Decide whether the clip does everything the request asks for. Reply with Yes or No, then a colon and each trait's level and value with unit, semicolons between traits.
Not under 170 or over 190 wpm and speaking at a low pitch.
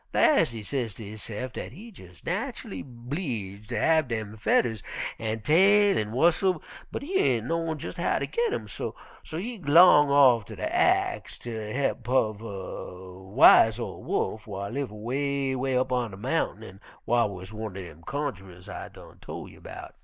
Yes: average, 175 wpm; low, 120 Hz